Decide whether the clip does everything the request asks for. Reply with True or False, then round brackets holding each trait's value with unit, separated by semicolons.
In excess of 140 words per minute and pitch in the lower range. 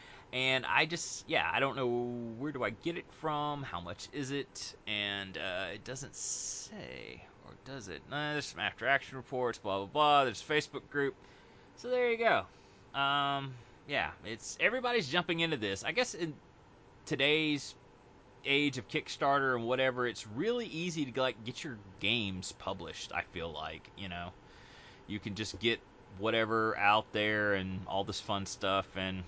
True (175 wpm; 125 Hz)